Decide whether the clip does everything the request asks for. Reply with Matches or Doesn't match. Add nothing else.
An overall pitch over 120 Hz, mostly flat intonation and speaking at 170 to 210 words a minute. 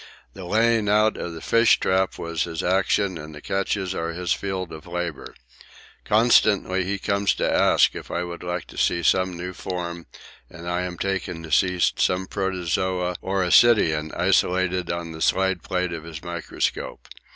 Doesn't match